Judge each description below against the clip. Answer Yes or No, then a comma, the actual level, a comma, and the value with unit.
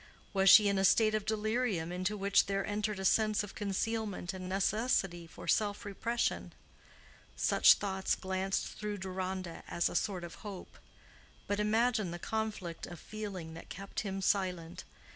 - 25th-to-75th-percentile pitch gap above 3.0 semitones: No, narrow, 2.4 semitones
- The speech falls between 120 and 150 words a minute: No, average, 160 wpm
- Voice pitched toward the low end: No, high, 195 Hz